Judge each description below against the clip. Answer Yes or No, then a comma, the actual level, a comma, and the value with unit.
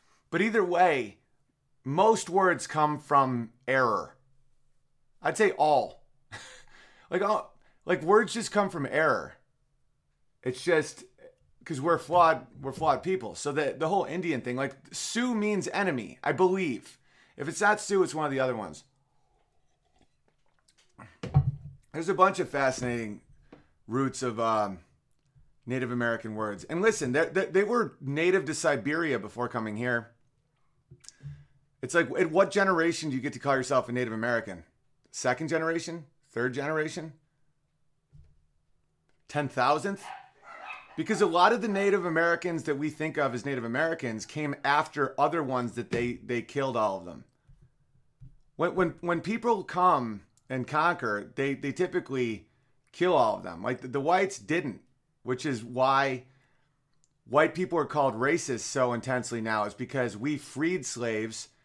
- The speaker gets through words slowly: No, average, 145 wpm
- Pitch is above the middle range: No, medium, 140 Hz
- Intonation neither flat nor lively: Yes, average, 4.9 semitones